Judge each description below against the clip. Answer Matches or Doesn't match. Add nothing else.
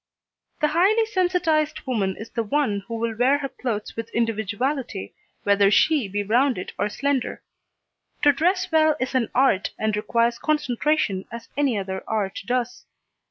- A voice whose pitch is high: Matches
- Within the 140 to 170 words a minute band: Matches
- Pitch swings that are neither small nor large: Doesn't match